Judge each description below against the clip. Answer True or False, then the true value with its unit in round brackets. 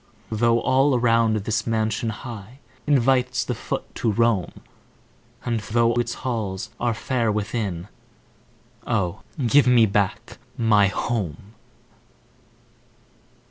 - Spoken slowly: True (105 wpm)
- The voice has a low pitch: True (115 Hz)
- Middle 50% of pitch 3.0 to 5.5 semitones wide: False (2.5 semitones)